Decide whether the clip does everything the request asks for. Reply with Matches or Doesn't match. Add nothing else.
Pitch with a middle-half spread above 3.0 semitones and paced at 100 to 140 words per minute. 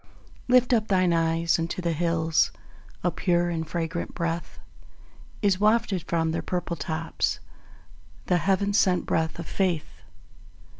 Doesn't match